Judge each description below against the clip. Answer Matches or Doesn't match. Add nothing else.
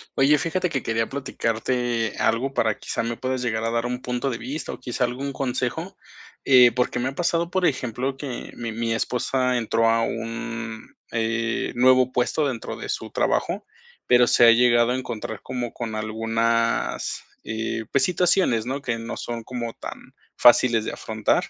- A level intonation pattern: Matches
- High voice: Doesn't match